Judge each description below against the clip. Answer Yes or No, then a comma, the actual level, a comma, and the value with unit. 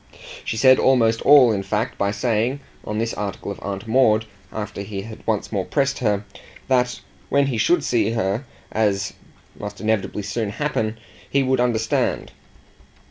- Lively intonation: No, average, 3.4 semitones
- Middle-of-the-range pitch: No, low, 110 Hz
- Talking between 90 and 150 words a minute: No, average, 160 wpm